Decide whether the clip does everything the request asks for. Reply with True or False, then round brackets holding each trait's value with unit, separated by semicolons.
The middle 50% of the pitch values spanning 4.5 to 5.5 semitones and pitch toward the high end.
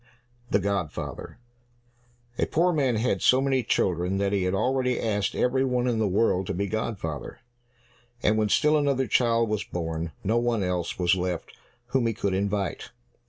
False (4.8 semitones; 105 Hz)